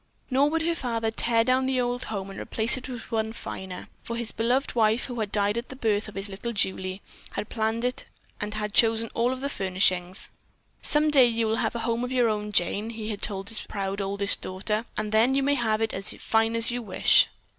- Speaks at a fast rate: Yes, fast, 230 wpm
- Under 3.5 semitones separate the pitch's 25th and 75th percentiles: Yes, average, 2.8 semitones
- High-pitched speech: Yes, high, 225 Hz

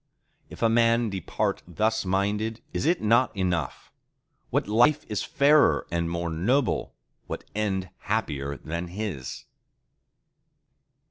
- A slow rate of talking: Yes, slow, 120 wpm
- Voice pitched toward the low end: Yes, low, 105 Hz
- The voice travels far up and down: No, average, 4.8 semitones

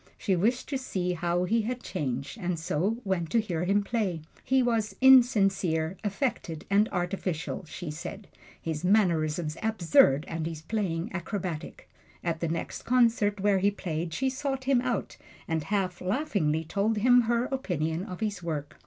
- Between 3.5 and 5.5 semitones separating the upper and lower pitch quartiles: Yes, average, 5.2 semitones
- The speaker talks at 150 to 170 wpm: Yes, average, 160 wpm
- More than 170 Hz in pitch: Yes, high, 190 Hz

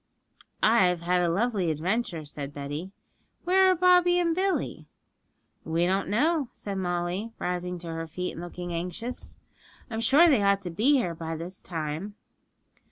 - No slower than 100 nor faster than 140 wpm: No, average, 160 wpm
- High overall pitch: No, medium, 180 Hz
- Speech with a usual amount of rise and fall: No, wide, 6.0 semitones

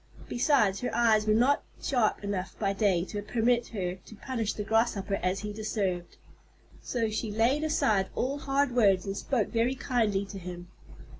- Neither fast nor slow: Yes, average, 170 wpm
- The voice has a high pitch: Yes, high, 215 Hz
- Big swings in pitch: No, average, 3.6 semitones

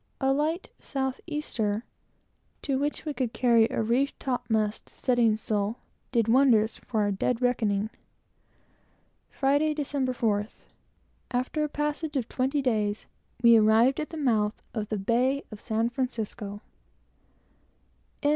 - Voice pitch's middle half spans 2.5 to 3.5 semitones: No, average, 4.0 semitones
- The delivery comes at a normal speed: No, slow, 130 wpm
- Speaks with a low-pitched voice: No, high, 245 Hz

